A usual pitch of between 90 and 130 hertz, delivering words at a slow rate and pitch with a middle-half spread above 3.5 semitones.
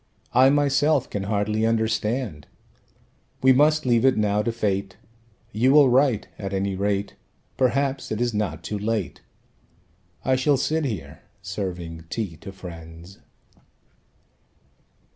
Yes: low, 110 Hz; slow, 125 wpm; average, 5.0 semitones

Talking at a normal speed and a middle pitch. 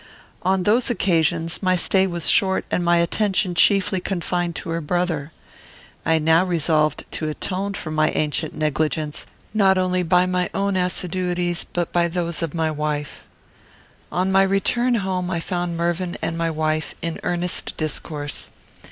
Yes: average, 155 wpm; medium, 175 Hz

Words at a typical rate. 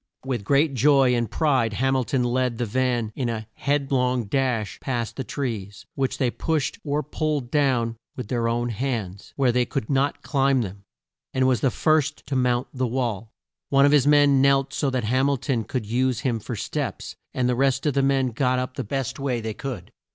No: fast, 210 wpm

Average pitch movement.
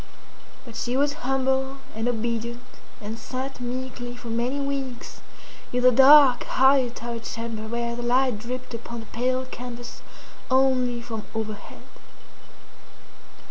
No: narrow, 1.9 semitones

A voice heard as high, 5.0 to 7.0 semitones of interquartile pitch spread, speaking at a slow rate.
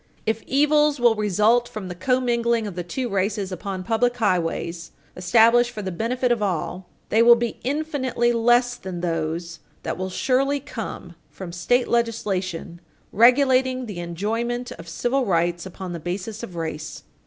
No: high, 220 Hz; average, 5.3 semitones; average, 155 wpm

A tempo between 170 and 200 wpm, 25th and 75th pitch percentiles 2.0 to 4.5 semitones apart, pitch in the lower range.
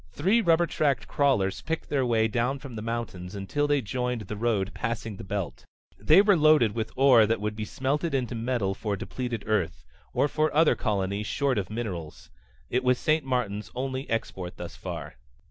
No: average, 185 wpm; average, 4.9 semitones; low, 120 Hz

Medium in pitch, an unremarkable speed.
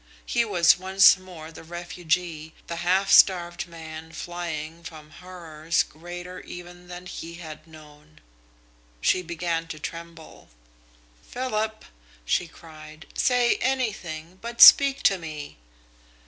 No: medium, 170 Hz; slow, 120 wpm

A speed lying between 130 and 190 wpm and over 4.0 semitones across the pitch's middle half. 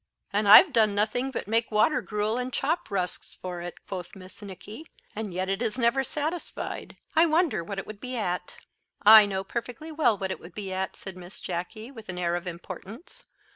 No: fast, 205 wpm; average, 4.6 semitones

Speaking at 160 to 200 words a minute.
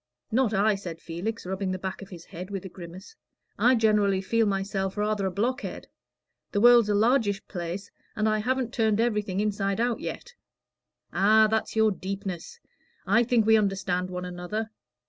Yes: average, 170 wpm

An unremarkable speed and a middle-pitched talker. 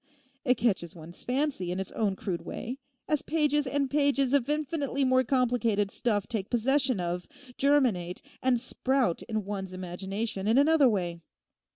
No: average, 155 wpm; high, 240 Hz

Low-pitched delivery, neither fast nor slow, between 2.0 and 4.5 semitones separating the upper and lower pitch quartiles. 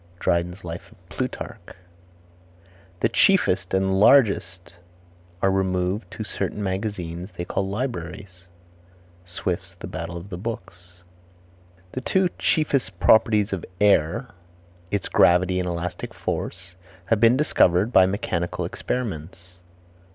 No: very low, 95 Hz; slow, 115 wpm; average, 3.4 semitones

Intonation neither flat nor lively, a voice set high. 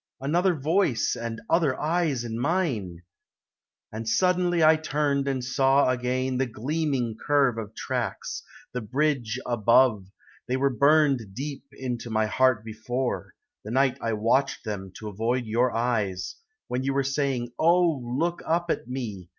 No: average, 4.1 semitones; low, 130 Hz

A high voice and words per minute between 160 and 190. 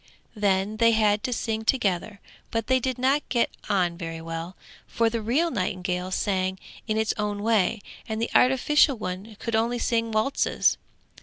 Yes: high, 220 Hz; average, 165 wpm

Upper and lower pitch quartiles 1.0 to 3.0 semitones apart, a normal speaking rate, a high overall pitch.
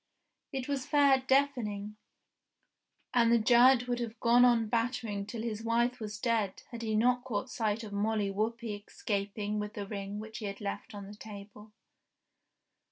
Yes: average, 2.7 semitones; average, 165 wpm; high, 220 Hz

